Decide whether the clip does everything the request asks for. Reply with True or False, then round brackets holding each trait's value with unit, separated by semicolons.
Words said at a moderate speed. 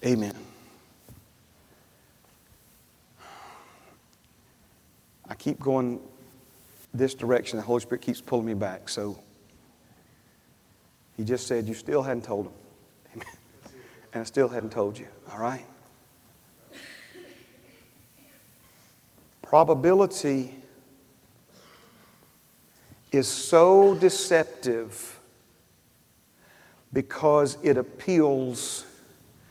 False (75 wpm)